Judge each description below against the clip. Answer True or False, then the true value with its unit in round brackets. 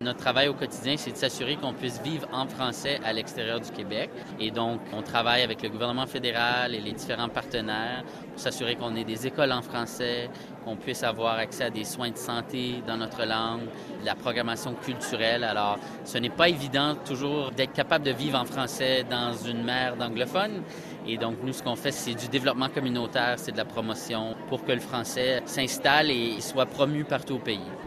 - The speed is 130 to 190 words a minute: False (200 wpm)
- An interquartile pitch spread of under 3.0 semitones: True (2.4 semitones)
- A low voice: True (125 Hz)